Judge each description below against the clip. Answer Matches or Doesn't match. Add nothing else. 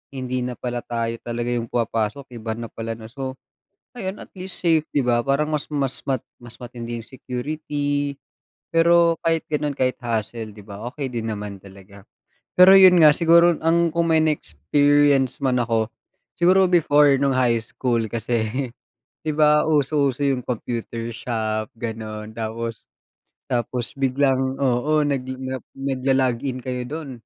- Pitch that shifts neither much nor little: Matches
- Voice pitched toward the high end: Doesn't match